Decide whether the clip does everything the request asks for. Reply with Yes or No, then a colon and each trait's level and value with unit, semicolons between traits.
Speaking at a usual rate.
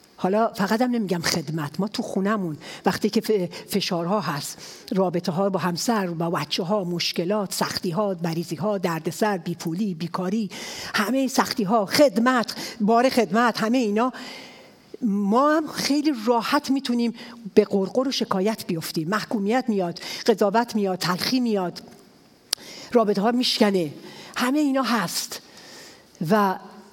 No: slow, 130 wpm